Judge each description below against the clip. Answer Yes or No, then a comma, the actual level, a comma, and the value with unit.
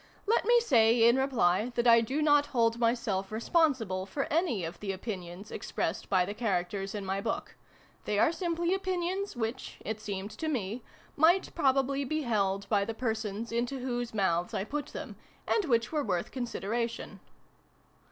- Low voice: No, high, 230 Hz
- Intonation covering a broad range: Yes, wide, 5.7 semitones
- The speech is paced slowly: No, average, 170 wpm